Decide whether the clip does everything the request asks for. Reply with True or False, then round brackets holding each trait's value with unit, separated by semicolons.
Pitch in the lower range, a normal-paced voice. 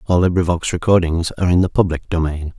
True (85 Hz; 185 wpm)